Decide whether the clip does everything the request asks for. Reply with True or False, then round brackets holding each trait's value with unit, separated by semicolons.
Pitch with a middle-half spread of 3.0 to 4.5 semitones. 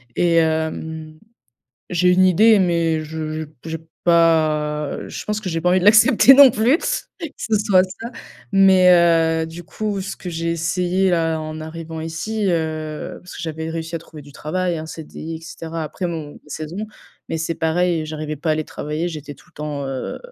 False (2.6 semitones)